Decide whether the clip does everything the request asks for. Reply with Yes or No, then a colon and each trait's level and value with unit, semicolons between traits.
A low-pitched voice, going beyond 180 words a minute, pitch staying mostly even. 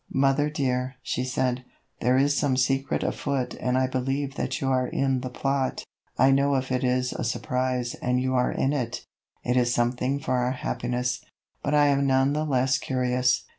Yes: low, 130 Hz; average, 190 wpm; narrow, 1.4 semitones